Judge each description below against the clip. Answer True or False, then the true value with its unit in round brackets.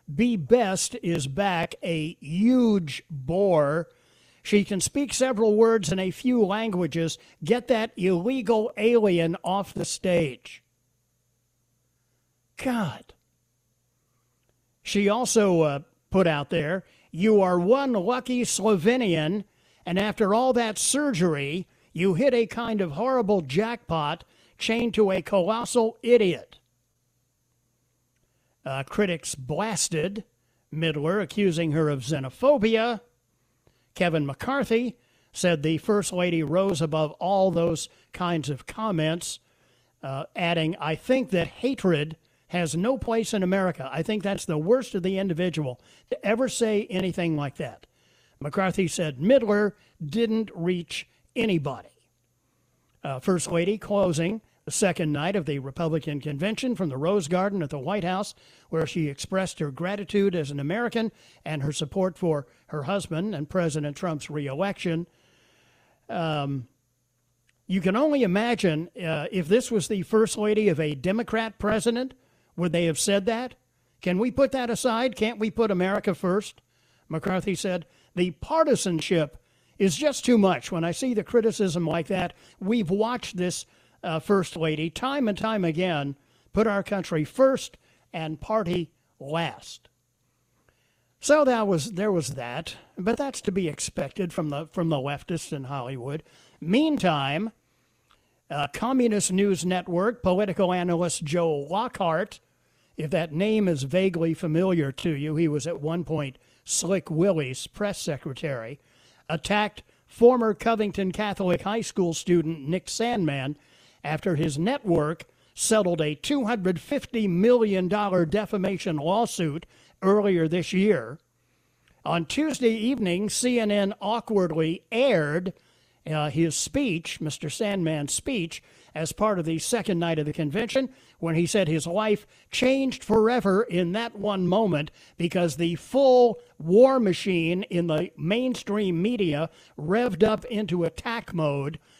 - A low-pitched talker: False (180 Hz)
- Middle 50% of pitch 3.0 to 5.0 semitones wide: False (5.5 semitones)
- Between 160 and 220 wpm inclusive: False (135 wpm)